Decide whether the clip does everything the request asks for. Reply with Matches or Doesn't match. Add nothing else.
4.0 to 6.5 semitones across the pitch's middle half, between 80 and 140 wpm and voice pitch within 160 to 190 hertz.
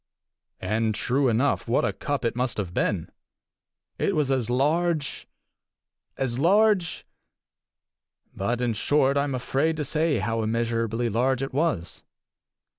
Doesn't match